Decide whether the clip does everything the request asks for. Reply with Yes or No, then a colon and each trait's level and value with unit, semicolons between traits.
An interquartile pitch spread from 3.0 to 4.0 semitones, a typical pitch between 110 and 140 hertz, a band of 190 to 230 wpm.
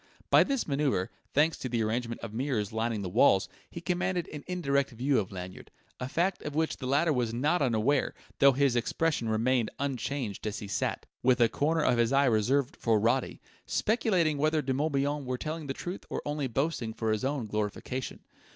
No: average, 4.6 semitones; low, 135 Hz; average, 195 wpm